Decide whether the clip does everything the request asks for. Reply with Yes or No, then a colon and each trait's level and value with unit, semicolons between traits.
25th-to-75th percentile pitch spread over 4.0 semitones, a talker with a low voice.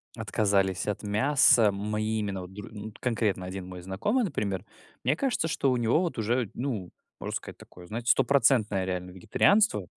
Yes: average, 4.6 semitones; low, 105 Hz